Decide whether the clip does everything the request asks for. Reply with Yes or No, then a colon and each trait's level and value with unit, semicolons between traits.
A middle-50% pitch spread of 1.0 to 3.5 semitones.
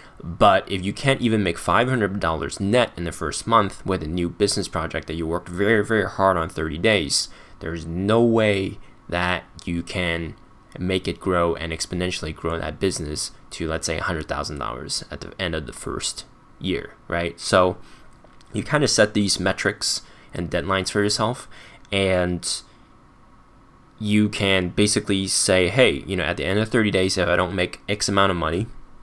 Yes: average, 3.2 semitones